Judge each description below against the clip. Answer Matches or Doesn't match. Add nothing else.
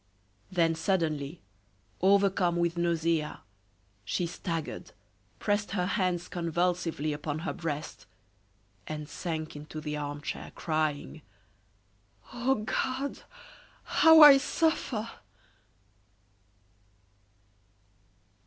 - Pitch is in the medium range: Matches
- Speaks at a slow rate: Matches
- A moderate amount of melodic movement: Matches